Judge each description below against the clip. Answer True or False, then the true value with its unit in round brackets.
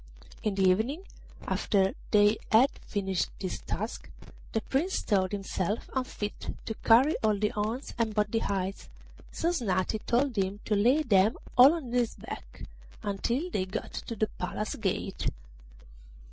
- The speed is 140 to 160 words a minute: True (150 wpm)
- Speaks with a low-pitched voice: False (215 Hz)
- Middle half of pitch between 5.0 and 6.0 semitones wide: False (3.8 semitones)